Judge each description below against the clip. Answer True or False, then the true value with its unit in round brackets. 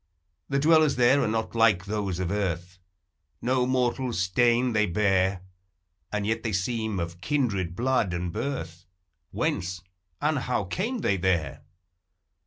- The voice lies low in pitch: True (105 Hz)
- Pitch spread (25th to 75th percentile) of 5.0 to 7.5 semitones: True (5.5 semitones)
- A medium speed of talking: True (150 wpm)